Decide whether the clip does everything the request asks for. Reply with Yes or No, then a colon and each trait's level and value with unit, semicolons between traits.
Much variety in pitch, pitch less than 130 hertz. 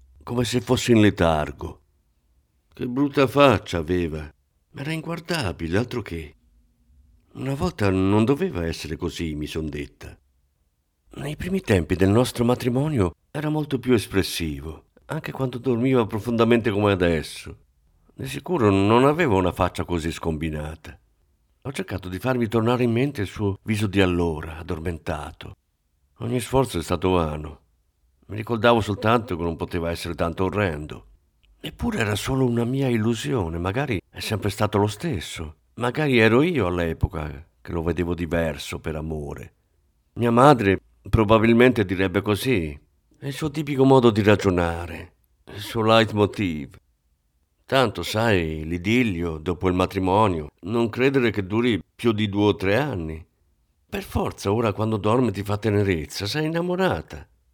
Yes: wide, 6.4 semitones; very low, 95 Hz